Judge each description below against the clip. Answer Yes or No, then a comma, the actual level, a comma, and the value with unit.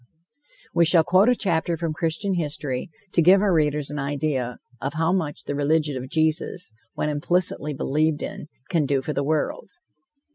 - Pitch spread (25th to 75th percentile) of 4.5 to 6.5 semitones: No, average, 2.8 semitones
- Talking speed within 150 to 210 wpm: Yes, average, 175 wpm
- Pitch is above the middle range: No, medium, 155 Hz